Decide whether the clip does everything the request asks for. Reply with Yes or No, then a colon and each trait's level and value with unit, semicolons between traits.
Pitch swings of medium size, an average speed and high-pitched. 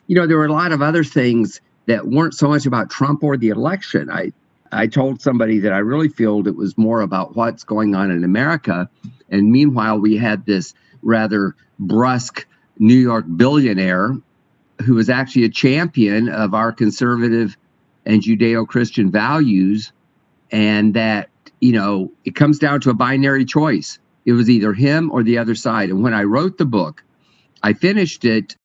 No: average, 4.0 semitones; average, 180 wpm; low, 115 Hz